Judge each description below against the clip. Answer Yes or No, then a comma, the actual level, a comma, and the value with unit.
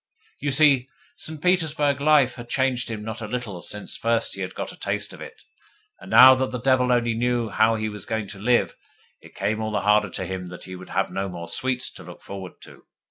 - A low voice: Yes, low, 115 Hz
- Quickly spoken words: Yes, fast, 235 wpm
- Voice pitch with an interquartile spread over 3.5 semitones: Yes, average, 4.0 semitones